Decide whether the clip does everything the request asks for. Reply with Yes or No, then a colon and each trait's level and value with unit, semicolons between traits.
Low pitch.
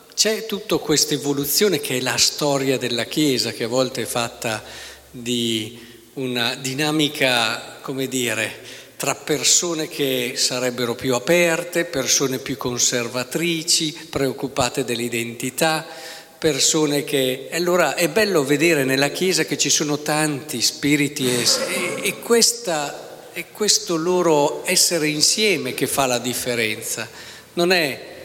No: medium, 145 Hz